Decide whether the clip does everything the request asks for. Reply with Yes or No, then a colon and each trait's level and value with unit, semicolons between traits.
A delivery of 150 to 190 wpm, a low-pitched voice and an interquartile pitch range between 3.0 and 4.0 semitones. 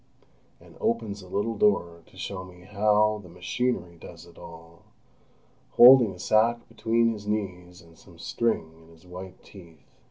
Yes: average, 160 wpm; very low, 95 Hz; average, 3.7 semitones